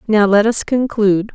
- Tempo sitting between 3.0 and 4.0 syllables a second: No, 5.0 syllables/s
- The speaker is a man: No, female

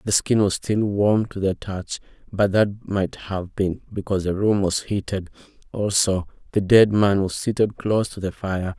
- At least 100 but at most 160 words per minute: No, average, 190 wpm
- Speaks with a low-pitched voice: Yes, low, 100 Hz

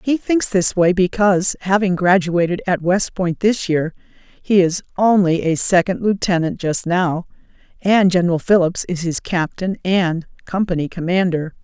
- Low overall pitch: No, medium, 180 Hz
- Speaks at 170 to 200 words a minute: No, average, 150 wpm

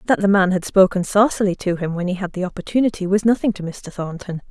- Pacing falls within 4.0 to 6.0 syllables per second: No, 6.2 syllables/s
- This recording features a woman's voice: Yes, female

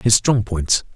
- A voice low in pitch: Yes, low, 105 Hz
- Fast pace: No, average, 190 wpm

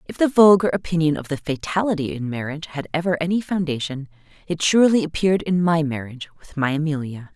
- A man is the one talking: No, female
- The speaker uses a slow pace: No, average, 180 wpm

